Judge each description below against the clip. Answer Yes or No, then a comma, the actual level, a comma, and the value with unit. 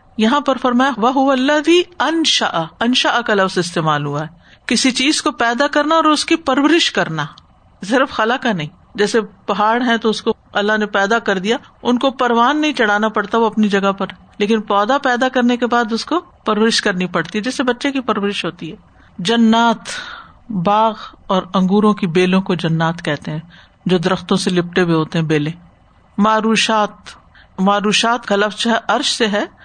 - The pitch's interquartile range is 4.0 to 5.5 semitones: Yes, average, 4.6 semitones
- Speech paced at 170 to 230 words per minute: Yes, average, 185 wpm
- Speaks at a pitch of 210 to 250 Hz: Yes, high, 220 Hz